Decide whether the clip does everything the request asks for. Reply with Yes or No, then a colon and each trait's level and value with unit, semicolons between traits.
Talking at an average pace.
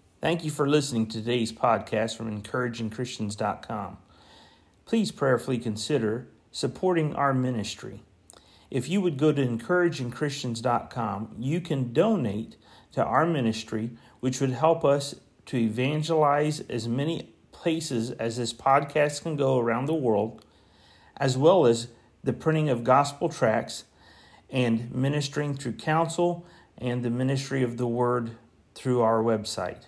No: slow, 130 wpm